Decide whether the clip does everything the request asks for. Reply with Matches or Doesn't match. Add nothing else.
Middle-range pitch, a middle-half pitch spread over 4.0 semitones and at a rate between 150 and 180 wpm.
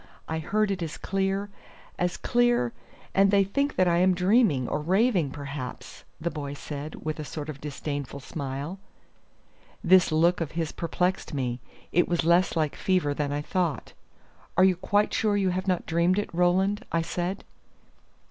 Matches